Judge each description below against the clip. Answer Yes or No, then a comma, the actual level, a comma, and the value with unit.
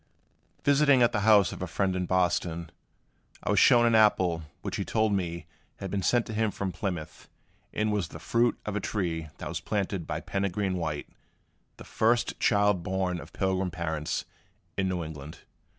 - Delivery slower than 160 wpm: No, average, 180 wpm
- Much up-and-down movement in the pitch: No, average, 3.7 semitones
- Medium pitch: No, very low, 95 Hz